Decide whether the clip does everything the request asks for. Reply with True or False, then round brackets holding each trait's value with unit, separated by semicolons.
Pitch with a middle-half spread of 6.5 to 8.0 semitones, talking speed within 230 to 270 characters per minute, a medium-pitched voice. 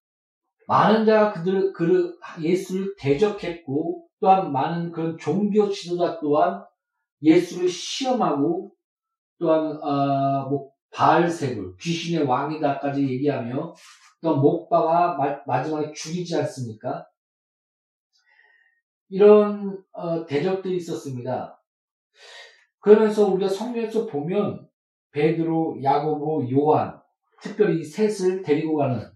False (5.9 semitones; 235 characters per minute; 170 Hz)